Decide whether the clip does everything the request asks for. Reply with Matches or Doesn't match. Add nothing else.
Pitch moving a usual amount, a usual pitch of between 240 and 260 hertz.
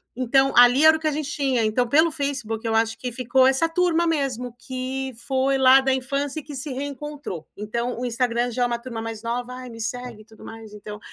Matches